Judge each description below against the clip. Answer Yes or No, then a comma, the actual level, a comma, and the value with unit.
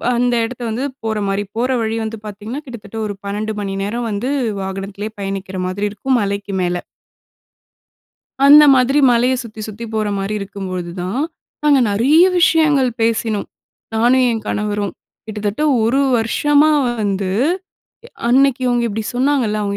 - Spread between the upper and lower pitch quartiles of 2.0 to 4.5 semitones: Yes, average, 3.8 semitones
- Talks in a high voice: Yes, high, 220 Hz